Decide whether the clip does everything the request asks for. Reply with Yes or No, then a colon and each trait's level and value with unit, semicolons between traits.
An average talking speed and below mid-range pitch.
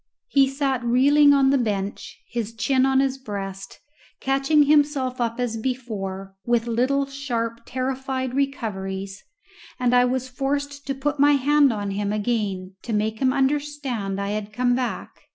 No: average, 155 wpm; very high, 255 Hz